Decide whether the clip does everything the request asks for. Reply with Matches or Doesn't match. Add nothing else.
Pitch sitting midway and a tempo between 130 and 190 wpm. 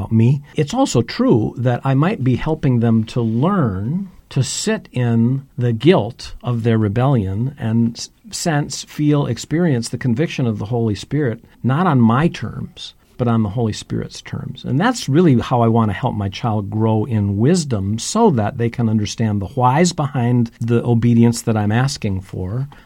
Doesn't match